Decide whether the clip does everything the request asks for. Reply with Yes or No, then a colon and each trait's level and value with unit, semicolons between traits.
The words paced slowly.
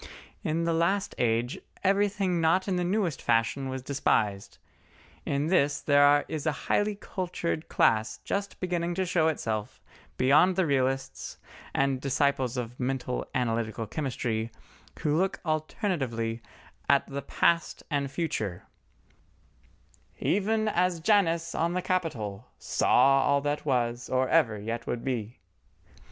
Yes: slow, 130 wpm